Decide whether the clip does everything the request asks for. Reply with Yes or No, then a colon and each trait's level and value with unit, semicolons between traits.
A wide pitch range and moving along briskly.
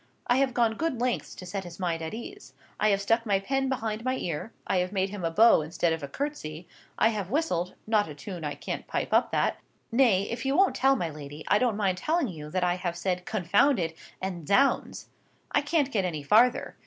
Yes: wide, 6.0 semitones; fast, 225 wpm